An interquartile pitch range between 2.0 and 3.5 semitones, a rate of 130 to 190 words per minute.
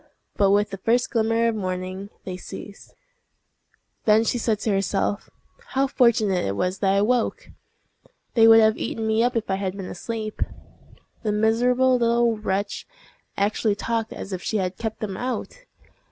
Yes: average, 2.8 semitones; average, 170 wpm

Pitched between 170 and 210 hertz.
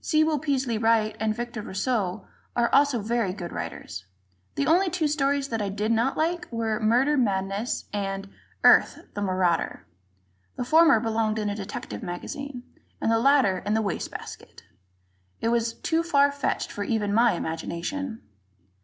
No: high, 225 Hz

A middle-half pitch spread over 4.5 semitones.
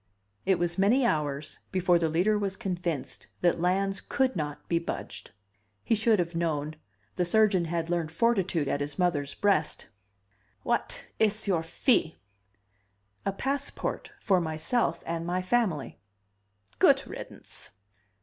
No: average, 3.7 semitones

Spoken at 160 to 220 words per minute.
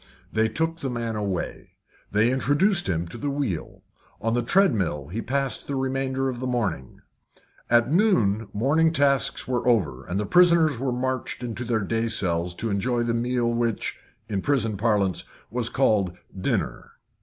Yes: average, 165 wpm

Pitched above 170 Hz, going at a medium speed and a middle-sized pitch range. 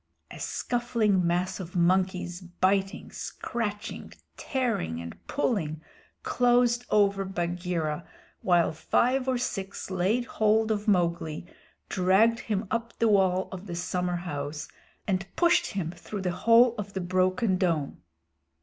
No: high, 190 Hz; slow, 125 wpm; average, 4.0 semitones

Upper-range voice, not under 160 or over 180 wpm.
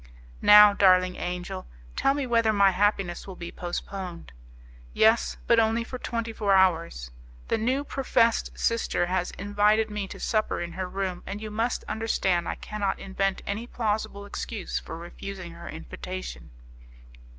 No: high, 200 Hz; average, 150 wpm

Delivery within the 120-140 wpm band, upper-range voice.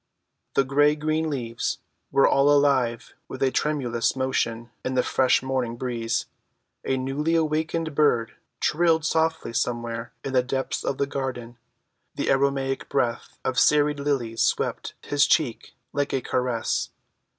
No: slow, 135 wpm; low, 135 Hz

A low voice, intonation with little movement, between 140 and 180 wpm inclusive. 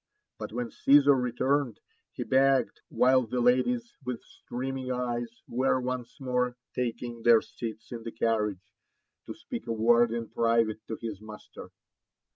Yes: low, 120 Hz; narrow, 1.9 semitones; average, 145 wpm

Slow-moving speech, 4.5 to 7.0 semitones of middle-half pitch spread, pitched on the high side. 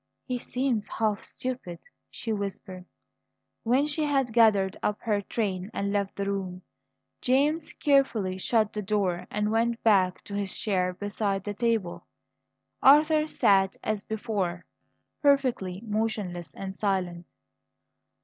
No: slow, 130 wpm; average, 3.6 semitones; high, 210 Hz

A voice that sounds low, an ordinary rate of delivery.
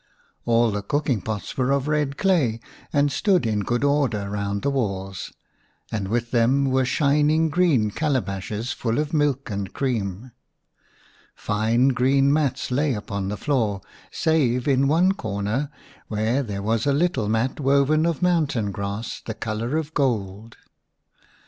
Yes: low, 125 Hz; average, 150 wpm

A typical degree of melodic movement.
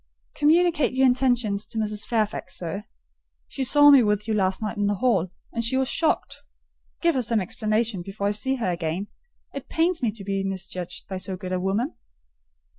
Yes: average, 5.0 semitones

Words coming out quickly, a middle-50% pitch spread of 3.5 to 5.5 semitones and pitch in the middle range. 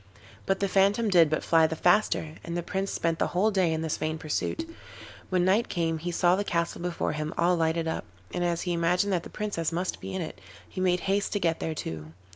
No: fast, 240 wpm; average, 2.7 semitones; medium, 175 Hz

